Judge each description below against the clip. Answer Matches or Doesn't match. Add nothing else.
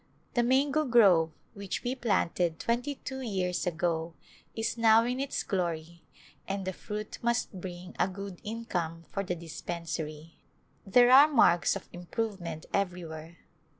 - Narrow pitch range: Doesn't match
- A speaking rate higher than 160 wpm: Doesn't match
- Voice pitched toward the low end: Doesn't match